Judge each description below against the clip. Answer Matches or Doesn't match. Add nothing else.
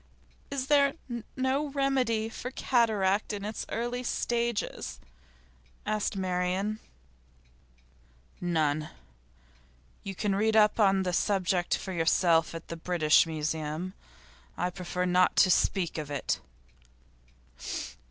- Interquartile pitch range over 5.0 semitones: Doesn't match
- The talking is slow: Matches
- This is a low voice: Doesn't match